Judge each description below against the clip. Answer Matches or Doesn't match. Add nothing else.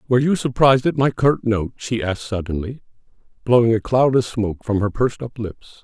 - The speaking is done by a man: Matches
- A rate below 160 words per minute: Doesn't match